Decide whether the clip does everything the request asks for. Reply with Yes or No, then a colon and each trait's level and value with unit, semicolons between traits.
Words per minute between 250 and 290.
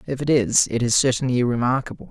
No: average, 200 wpm